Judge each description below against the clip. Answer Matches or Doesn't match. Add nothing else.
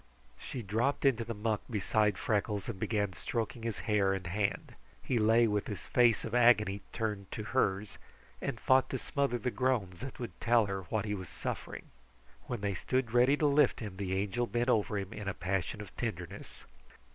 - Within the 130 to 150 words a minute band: Doesn't match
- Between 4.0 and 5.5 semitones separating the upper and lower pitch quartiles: Doesn't match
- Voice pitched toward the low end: Matches